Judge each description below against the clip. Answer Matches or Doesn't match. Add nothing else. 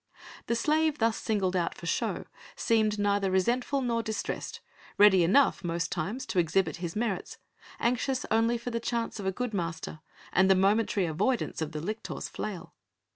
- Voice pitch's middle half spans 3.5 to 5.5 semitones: Matches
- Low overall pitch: Doesn't match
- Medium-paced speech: Matches